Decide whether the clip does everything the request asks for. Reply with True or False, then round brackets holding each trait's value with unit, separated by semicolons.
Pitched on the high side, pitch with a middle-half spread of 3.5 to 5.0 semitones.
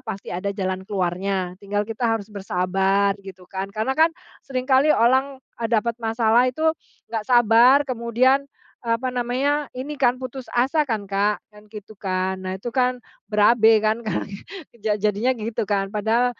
True (225 Hz; 4.0 semitones)